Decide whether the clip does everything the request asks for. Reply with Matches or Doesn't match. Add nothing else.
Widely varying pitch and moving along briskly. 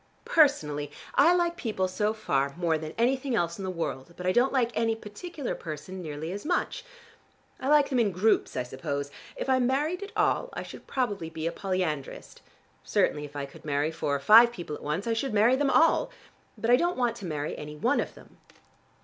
Matches